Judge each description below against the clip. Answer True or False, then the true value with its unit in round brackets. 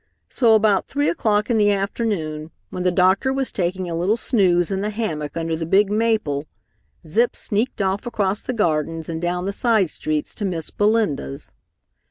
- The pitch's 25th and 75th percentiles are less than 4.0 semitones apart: False (4.7 semitones)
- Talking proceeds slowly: False (180 wpm)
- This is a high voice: True (195 Hz)